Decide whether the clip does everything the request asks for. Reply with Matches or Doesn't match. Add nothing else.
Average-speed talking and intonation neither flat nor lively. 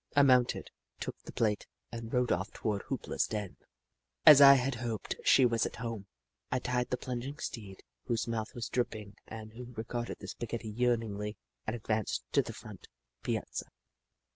Doesn't match